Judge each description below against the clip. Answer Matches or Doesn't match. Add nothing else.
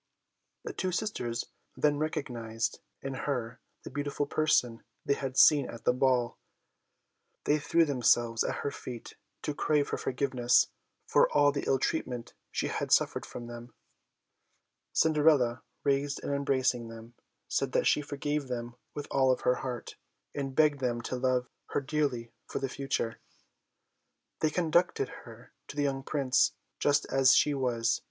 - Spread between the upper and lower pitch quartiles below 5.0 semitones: Matches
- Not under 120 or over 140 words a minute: Doesn't match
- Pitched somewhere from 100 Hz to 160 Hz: Matches